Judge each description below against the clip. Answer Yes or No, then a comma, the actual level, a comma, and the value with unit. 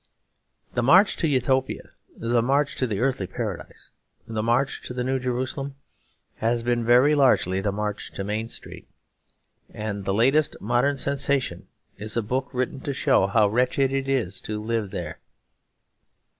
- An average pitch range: Yes, average, 3.9 semitones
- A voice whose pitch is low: Yes, low, 120 Hz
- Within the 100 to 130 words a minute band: No, average, 155 wpm